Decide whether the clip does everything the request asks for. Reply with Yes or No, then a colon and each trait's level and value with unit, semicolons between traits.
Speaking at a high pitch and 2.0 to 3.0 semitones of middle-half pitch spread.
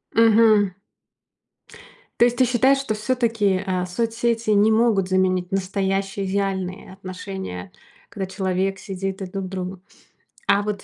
Yes: high, 195 Hz; average, 2.7 semitones